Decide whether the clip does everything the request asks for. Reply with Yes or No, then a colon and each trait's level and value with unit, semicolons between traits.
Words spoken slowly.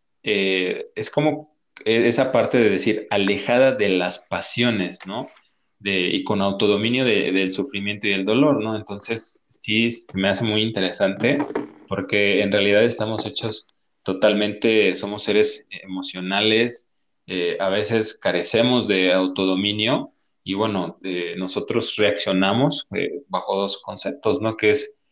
No: average, 135 wpm